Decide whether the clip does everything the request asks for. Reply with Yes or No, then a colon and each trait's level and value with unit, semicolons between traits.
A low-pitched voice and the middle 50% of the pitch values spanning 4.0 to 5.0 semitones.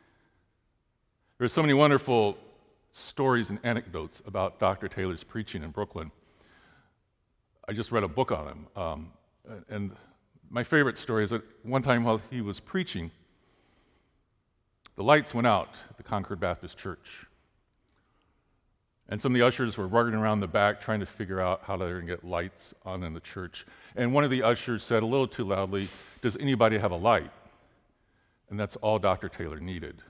Yes: low, 105 Hz; average, 4.3 semitones